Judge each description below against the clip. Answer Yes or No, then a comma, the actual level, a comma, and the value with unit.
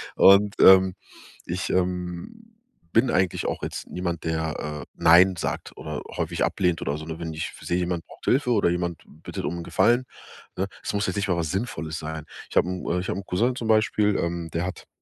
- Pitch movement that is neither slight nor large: Yes, average, 3.1 semitones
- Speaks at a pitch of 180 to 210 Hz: No, very low, 90 Hz